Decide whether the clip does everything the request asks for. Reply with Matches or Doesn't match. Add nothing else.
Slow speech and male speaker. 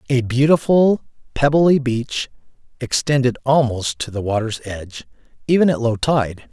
Matches